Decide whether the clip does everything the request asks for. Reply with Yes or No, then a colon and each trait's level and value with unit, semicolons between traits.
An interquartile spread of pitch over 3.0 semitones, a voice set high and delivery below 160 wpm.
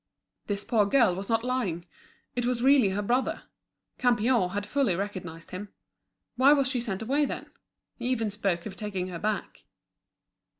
No: average, 4.5 semitones; high, 210 Hz; average, 165 wpm